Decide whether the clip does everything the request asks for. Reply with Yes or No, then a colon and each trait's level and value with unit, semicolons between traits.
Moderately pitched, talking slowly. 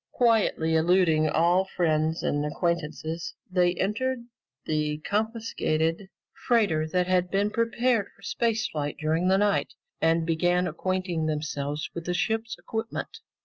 Yes: medium, 180 Hz; slow, 130 wpm